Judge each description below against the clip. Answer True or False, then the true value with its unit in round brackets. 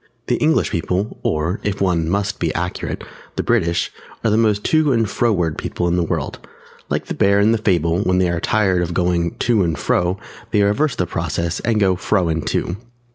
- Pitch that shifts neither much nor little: True (3.6 semitones)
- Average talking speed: False (215 wpm)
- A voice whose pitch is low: True (90 Hz)